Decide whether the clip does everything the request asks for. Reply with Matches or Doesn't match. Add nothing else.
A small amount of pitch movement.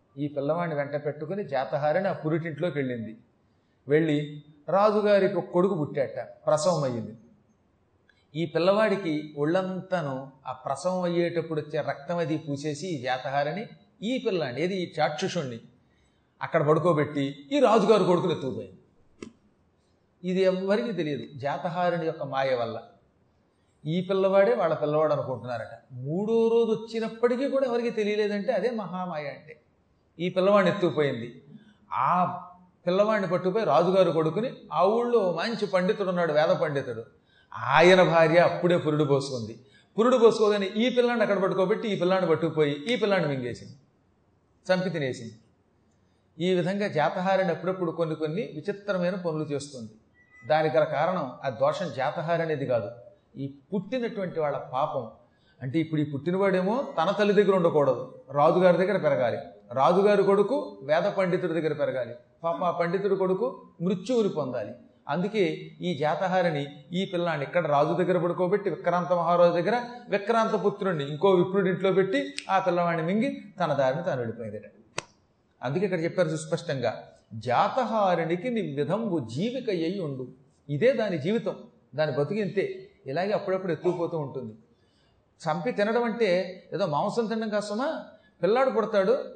Doesn't match